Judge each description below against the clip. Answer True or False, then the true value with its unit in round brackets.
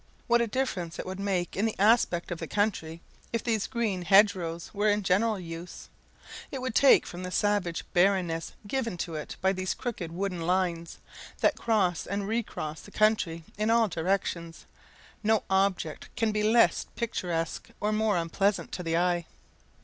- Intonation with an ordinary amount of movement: True (3.8 semitones)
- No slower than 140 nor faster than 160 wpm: False (170 wpm)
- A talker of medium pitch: False (195 Hz)